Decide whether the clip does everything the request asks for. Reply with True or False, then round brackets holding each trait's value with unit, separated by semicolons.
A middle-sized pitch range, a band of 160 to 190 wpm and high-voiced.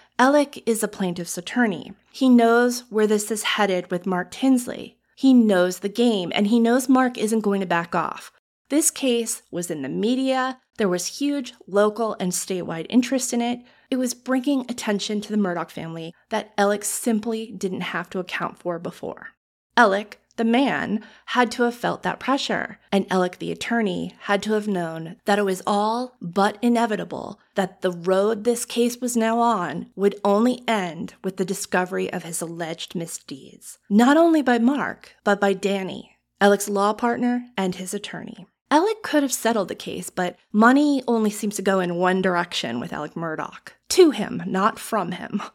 True (4.2 semitones; 180 wpm; 210 Hz)